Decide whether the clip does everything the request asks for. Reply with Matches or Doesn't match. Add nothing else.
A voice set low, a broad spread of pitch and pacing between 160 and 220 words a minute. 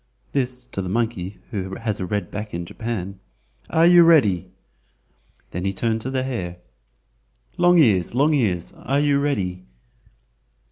Doesn't match